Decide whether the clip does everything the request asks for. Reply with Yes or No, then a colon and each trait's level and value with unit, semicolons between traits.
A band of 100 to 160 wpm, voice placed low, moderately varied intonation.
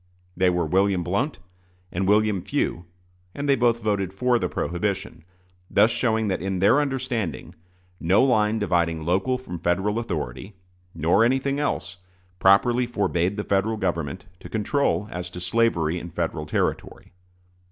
Yes: average, 145 wpm; low, 100 Hz; average, 4.8 semitones